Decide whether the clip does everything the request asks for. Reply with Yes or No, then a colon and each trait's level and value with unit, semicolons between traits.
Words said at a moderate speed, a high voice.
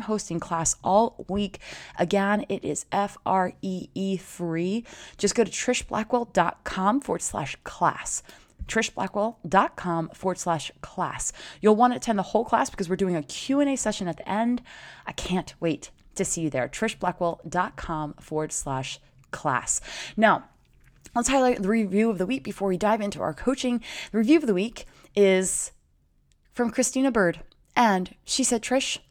Yes: average, 155 wpm; high, 195 Hz